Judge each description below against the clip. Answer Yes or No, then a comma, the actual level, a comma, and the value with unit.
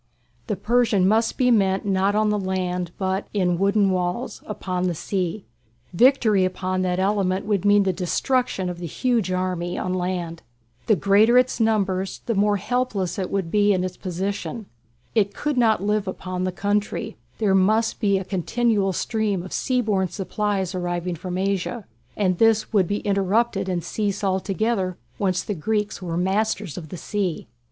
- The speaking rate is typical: Yes, average, 165 wpm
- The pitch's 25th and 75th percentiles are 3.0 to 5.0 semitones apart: No, narrow, 2.5 semitones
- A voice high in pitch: Yes, high, 195 Hz